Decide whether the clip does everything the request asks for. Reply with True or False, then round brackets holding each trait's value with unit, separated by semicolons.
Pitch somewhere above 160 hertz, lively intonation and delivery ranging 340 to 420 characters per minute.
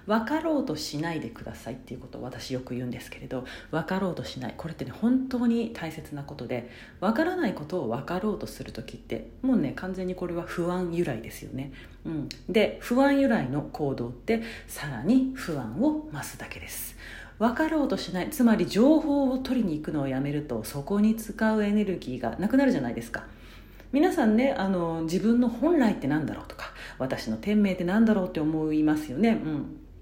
True (185 Hz; 8.4 semitones; 400 characters per minute)